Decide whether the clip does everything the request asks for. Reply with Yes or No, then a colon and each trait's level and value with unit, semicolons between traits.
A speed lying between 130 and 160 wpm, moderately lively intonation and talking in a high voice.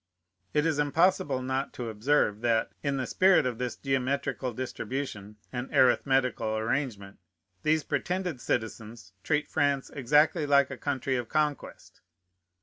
No: slow, 135 wpm; average, 3.4 semitones; low, 135 Hz